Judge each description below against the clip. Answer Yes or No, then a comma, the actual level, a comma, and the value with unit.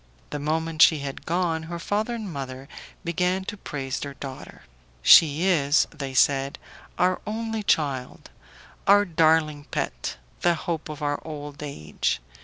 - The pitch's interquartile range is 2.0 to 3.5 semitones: No, average, 3.9 semitones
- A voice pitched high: No, medium, 155 Hz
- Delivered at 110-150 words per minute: Yes, average, 145 wpm